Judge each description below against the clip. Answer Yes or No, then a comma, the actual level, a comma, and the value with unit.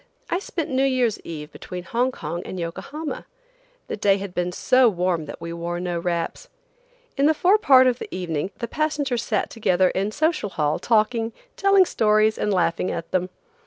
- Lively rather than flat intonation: Yes, wide, 6.8 semitones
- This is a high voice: Yes, high, 210 Hz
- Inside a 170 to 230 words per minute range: Yes, average, 180 wpm